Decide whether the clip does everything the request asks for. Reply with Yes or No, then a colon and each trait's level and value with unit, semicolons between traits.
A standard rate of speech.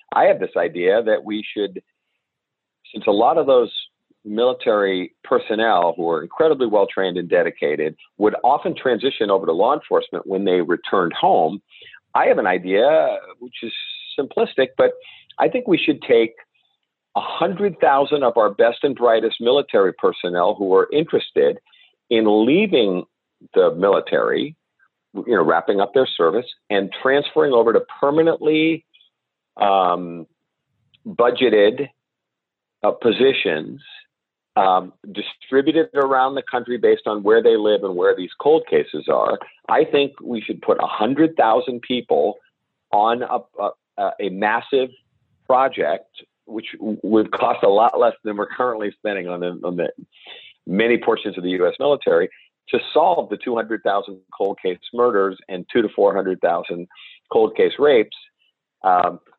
Yes: average, 145 wpm